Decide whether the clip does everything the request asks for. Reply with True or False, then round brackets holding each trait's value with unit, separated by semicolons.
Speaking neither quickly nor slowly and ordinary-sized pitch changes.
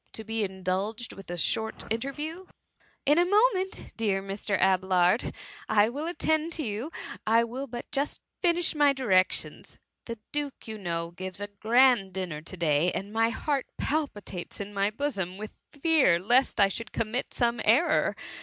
False (165 wpm; 6.4 semitones)